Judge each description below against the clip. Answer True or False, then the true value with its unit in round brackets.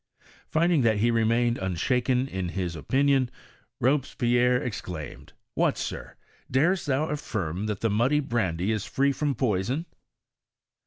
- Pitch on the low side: True (120 Hz)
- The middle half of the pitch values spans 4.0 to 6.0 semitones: True (5.1 semitones)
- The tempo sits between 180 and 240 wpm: False (140 wpm)